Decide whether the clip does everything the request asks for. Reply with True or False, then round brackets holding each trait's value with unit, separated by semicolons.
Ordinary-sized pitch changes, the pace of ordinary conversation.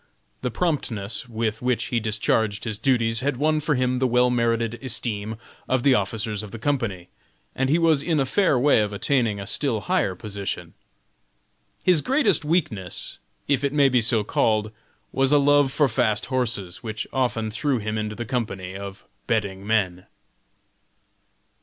True (4.1 semitones; 165 wpm)